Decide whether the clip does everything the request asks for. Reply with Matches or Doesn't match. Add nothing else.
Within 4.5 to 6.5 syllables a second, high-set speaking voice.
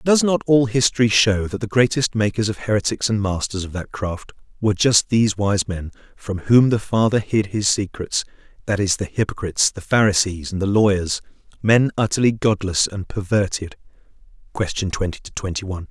Doesn't match